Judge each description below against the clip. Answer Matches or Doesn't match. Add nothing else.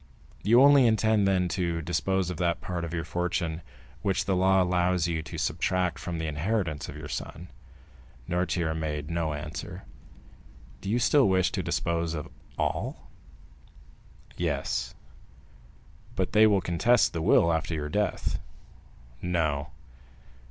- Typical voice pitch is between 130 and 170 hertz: Doesn't match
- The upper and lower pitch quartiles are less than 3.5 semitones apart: Matches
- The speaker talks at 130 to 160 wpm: Matches